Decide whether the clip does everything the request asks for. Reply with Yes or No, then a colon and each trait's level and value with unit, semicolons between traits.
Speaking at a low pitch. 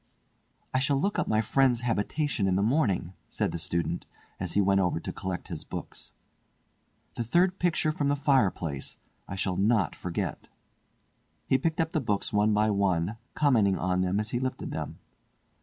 Yes: low, 105 Hz